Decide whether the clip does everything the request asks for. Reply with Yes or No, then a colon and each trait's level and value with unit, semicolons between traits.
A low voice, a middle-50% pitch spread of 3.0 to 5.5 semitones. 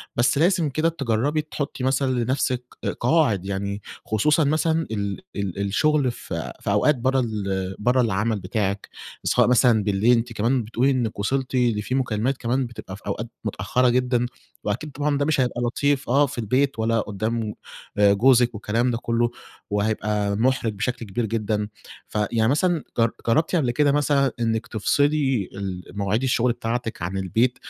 Yes: low, 120 Hz; average, 4.2 semitones